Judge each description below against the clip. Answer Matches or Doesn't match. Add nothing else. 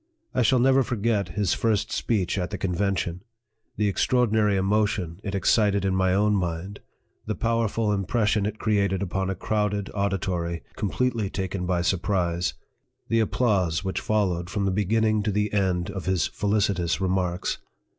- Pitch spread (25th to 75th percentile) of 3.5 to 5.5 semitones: Doesn't match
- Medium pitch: Doesn't match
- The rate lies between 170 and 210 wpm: Doesn't match